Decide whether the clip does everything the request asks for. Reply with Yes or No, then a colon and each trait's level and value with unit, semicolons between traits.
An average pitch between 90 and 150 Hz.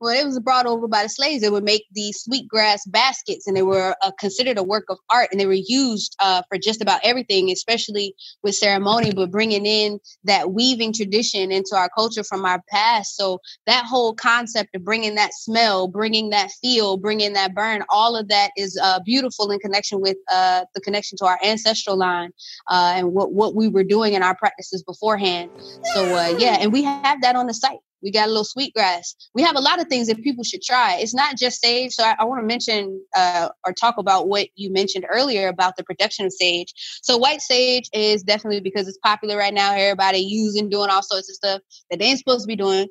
No: high, 210 Hz